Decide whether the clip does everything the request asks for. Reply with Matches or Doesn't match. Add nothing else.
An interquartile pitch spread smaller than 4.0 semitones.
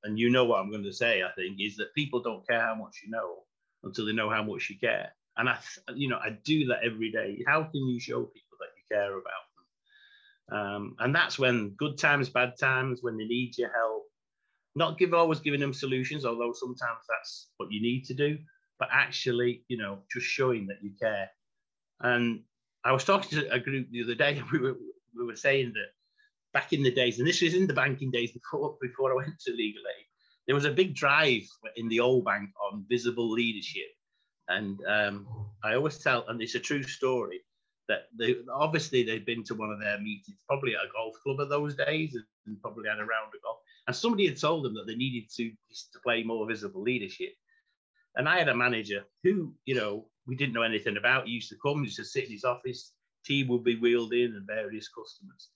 Doesn't match